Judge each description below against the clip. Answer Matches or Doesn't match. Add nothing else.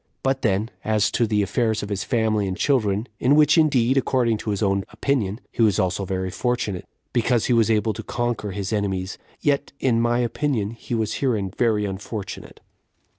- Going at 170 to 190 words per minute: Matches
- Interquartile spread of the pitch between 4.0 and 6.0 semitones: Doesn't match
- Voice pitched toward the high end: Doesn't match